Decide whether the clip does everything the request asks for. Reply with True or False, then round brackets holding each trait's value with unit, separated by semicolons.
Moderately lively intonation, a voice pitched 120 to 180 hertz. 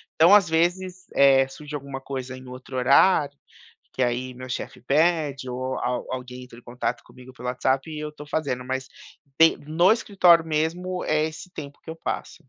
True (4.0 semitones; 140 Hz)